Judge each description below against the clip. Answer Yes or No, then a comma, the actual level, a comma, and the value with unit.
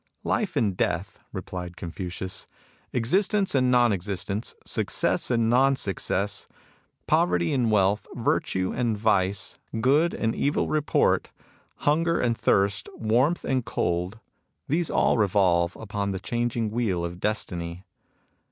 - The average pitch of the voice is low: Yes, low, 110 Hz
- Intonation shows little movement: No, average, 5.1 semitones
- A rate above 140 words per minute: No, slow, 135 wpm